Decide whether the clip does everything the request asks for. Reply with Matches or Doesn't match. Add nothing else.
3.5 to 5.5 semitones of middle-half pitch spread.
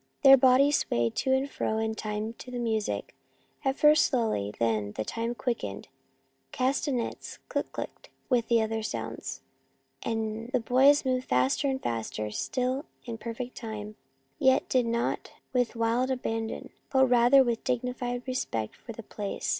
Doesn't match